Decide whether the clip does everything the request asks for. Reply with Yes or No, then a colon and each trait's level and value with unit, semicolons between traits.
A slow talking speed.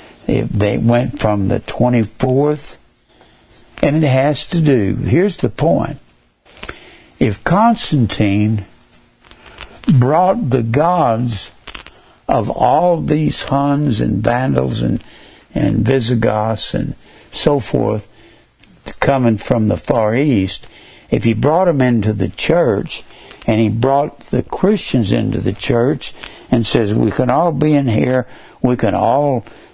Yes: slow, 125 wpm